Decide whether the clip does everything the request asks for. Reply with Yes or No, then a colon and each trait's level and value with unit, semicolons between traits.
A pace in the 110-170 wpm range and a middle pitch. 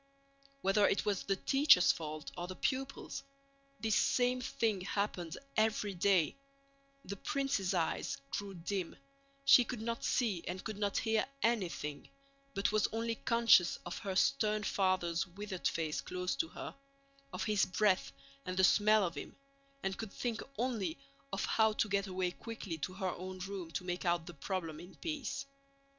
No: average, 165 wpm; high, 195 Hz